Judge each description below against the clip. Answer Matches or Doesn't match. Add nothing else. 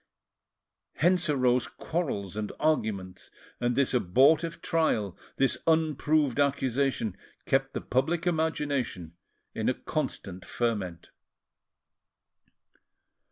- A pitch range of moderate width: Doesn't match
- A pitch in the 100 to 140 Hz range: Matches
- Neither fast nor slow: Doesn't match